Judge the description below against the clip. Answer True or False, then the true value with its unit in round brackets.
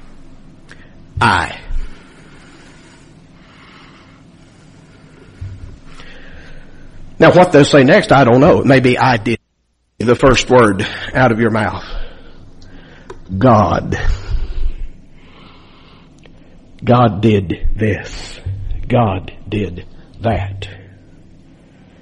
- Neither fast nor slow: False (70 wpm)